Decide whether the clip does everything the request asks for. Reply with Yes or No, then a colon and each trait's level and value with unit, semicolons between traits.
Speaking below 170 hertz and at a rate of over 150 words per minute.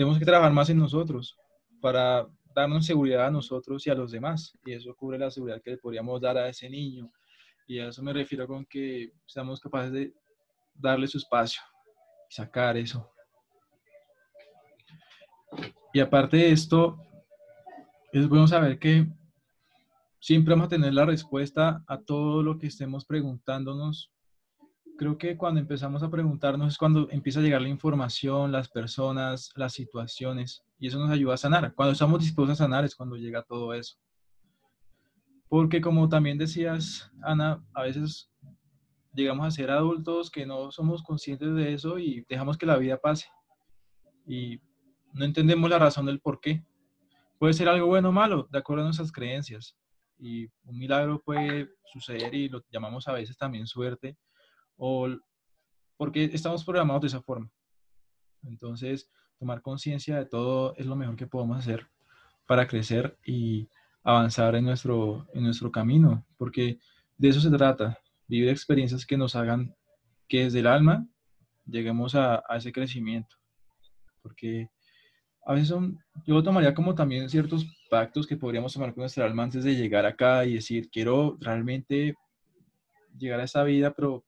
Yes: medium, 140 Hz; average, 160 wpm